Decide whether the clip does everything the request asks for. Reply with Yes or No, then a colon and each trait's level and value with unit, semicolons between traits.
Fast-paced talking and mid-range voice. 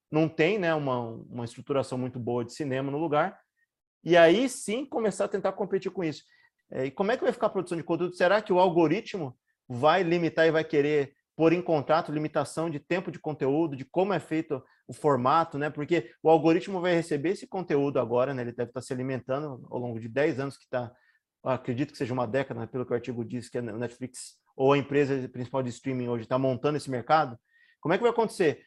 Yes: fast, 225 wpm; medium, 150 Hz